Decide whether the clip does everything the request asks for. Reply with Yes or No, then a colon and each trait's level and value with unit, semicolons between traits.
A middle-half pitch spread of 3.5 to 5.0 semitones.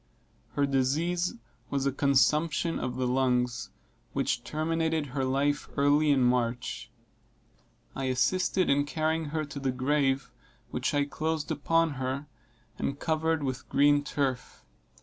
No: average, 3.0 semitones